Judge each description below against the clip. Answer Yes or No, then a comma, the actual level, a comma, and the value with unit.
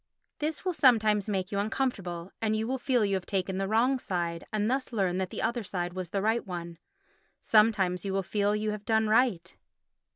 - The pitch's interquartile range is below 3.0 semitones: No, average, 3.3 semitones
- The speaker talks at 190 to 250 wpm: Yes, average, 200 wpm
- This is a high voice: Yes, high, 210 Hz